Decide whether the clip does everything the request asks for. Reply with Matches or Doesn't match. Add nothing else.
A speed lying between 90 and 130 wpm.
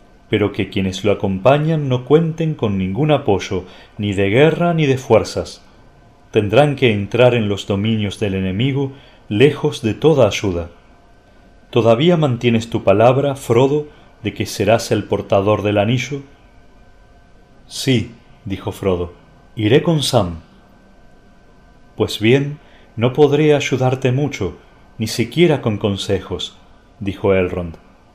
Matches